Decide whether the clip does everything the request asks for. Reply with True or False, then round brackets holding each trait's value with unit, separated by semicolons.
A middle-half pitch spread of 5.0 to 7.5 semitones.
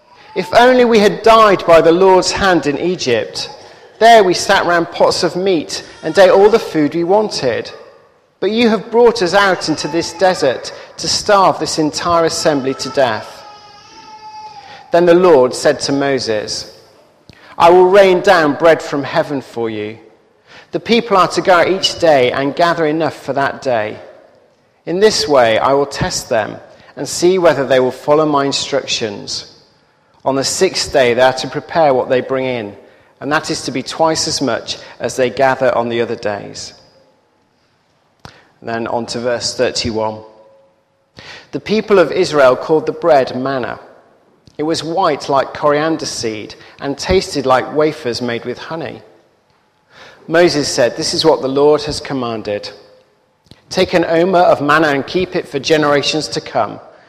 True (5.5 semitones)